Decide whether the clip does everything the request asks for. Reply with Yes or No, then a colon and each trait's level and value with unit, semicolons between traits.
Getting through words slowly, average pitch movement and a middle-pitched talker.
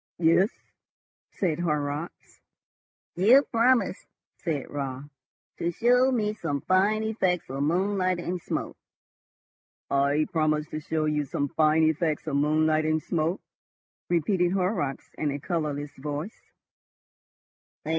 Yes: slow, 115 wpm; average, 3.8 semitones; medium, 160 Hz